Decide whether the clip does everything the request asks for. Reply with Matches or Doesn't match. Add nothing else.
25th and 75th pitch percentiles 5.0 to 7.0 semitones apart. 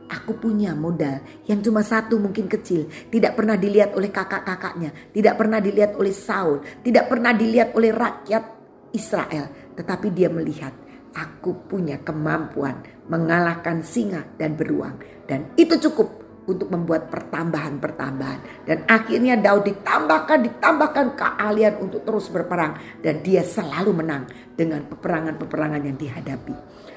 Matches